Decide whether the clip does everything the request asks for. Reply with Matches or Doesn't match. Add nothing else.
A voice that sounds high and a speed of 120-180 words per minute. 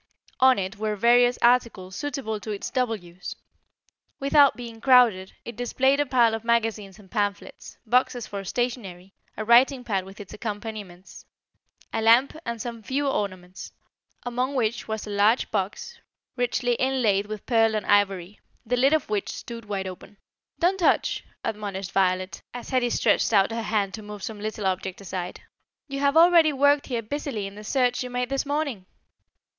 Matches